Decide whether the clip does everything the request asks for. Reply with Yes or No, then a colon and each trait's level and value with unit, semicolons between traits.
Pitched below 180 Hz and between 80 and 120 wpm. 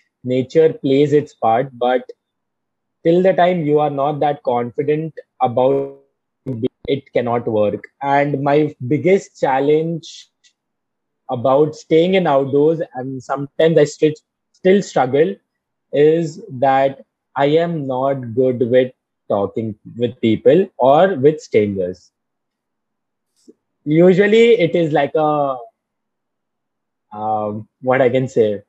Yes: medium, 140 Hz; average, 115 wpm